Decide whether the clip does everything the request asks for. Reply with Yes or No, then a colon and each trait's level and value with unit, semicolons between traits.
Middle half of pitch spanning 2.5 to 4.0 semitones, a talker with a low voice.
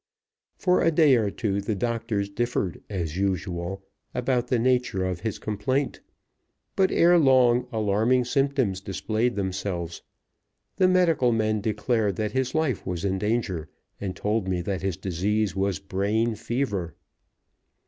No: average, 4.4 semitones; low, 105 Hz